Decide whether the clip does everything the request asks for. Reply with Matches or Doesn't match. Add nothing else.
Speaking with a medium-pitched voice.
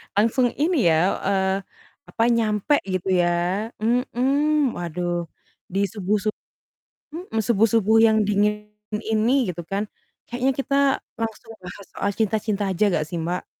Doesn't match